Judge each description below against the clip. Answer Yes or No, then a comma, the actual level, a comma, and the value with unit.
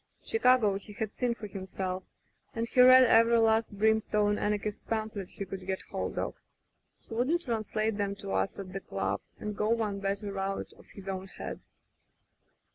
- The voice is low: No, high, 210 Hz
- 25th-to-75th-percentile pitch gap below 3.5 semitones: Yes, narrow, 2.4 semitones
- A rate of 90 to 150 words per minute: No, average, 180 wpm